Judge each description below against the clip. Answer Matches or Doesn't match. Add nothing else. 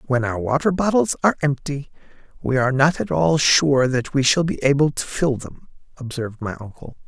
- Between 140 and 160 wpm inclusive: Doesn't match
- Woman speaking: Doesn't match